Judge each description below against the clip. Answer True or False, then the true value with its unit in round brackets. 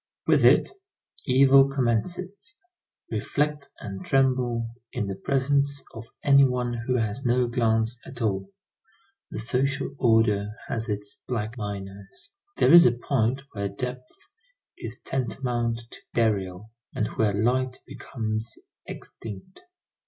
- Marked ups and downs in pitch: False (3.7 semitones)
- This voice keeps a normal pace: False (125 wpm)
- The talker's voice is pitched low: True (120 Hz)